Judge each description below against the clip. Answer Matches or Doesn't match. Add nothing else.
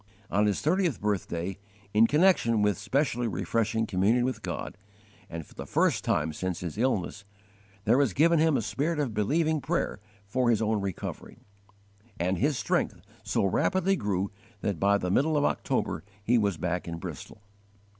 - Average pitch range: Doesn't match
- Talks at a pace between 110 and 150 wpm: Doesn't match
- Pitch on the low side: Matches